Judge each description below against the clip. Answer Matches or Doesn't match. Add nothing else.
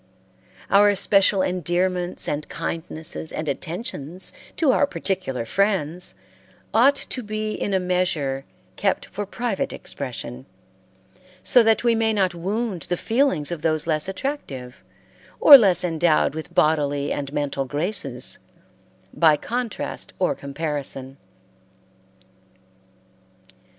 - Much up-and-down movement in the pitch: Matches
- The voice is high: Doesn't match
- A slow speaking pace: Matches